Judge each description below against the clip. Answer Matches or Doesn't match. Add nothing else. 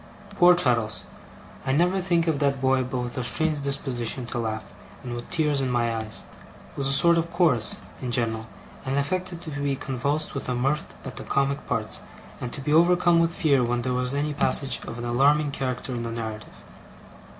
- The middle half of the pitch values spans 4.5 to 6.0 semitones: Doesn't match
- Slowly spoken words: Doesn't match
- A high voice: Doesn't match